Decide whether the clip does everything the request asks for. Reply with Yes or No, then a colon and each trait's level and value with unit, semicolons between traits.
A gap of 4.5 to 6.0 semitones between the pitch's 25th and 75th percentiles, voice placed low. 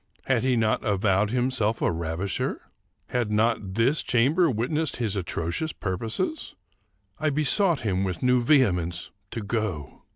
Yes: average, 5.2 semitones; low, 115 Hz